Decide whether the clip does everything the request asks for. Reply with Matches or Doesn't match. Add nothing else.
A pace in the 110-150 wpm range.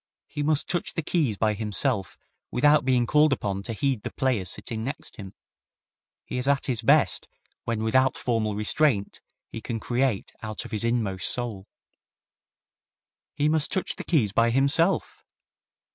Doesn't match